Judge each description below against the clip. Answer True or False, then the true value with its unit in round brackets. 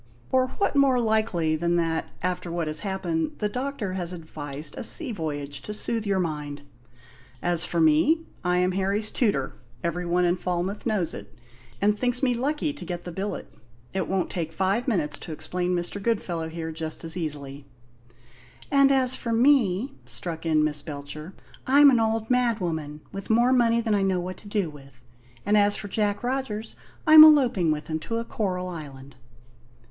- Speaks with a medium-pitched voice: True (180 Hz)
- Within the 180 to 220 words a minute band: True (185 wpm)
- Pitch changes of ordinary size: False (6.0 semitones)